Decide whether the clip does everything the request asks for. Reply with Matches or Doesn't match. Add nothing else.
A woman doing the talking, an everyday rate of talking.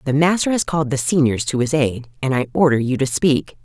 Doesn't match